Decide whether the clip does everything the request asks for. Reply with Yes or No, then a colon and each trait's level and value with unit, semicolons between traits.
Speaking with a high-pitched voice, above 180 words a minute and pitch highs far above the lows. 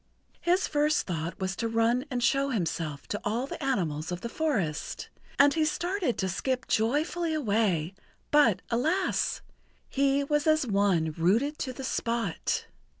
No: high, 240 Hz; average, 155 wpm; wide, 7.4 semitones